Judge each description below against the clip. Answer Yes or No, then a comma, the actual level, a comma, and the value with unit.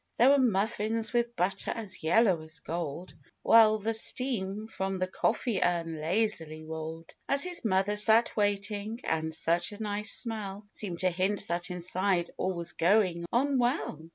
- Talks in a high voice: Yes, high, 195 Hz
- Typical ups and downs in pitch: Yes, average, 4.4 semitones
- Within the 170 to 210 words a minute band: No, average, 160 wpm